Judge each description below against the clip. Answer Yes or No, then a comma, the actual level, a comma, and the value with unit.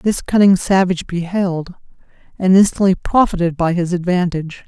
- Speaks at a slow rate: Yes, slow, 130 wpm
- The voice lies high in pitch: No, medium, 180 Hz